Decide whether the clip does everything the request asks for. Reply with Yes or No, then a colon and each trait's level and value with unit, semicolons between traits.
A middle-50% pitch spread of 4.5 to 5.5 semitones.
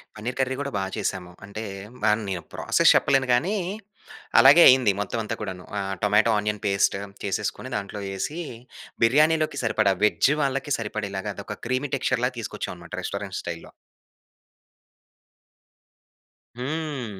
Yes: average, 5.0 semitones